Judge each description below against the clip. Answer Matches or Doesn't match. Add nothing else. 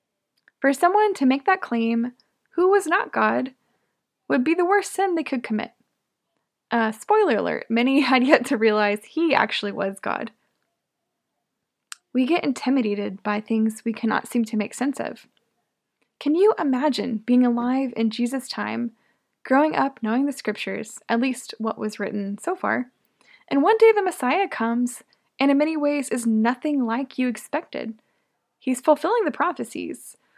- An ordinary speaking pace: Matches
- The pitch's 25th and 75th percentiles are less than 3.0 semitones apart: Doesn't match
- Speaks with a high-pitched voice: Matches